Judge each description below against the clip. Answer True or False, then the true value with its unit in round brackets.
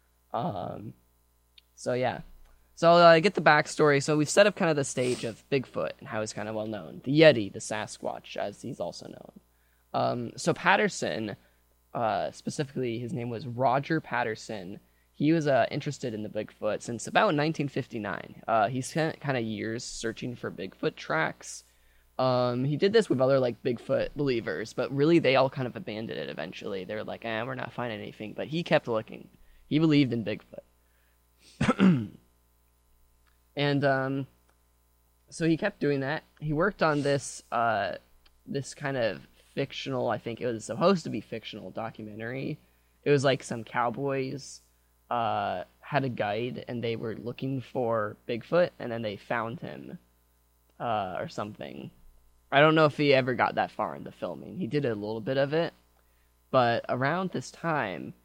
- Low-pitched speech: True (120 Hz)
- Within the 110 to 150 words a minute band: False (175 wpm)